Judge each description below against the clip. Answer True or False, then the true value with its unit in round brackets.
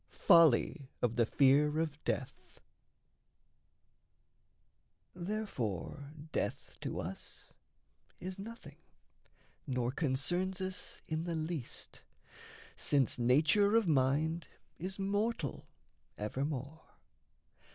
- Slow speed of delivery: True (85 wpm)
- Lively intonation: True (5.8 semitones)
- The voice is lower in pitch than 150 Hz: False (155 Hz)